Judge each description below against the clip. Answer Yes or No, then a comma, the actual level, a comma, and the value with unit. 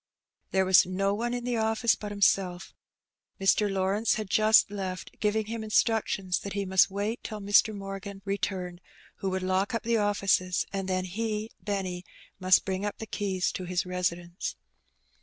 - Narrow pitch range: Yes, narrow, 2.3 semitones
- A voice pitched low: No, high, 195 Hz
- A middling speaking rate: Yes, average, 170 wpm